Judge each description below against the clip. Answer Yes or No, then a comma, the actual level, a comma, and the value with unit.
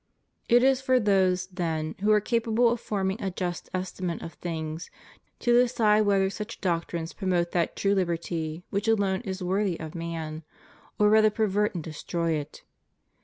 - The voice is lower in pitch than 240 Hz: Yes, high, 190 Hz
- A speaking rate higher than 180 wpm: No, average, 165 wpm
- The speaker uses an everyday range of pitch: Yes, average, 3.9 semitones